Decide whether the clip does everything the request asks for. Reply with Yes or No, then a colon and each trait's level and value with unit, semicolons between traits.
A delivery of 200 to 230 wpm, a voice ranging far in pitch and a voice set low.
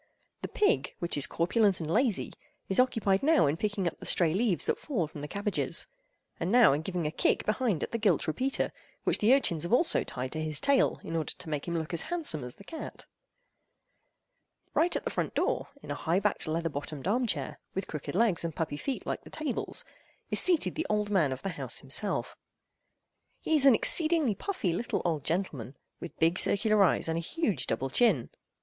No: fast, 205 wpm; wide, 6.9 semitones; medium, 185 Hz